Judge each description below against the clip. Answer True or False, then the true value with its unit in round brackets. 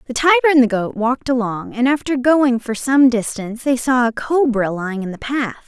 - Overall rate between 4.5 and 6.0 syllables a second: True (5.6 syllables/s)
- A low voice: False (250 Hz)